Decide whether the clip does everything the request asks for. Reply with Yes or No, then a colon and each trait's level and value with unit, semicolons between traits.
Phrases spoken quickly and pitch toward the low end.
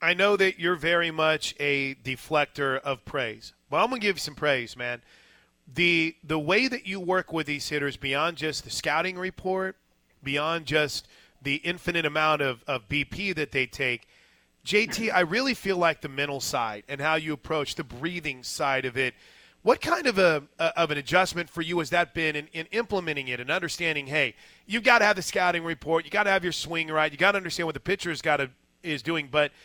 No: fast, 215 wpm; medium, 160 Hz